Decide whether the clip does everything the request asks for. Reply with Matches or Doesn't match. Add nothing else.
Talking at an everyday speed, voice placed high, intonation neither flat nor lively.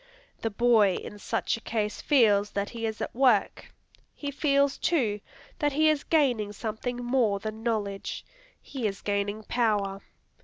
Matches